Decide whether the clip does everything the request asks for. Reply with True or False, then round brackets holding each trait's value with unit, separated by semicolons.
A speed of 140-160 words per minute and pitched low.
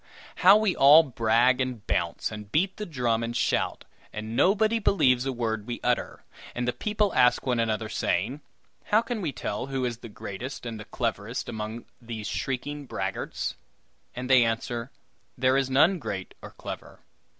False (175 wpm; 125 Hz)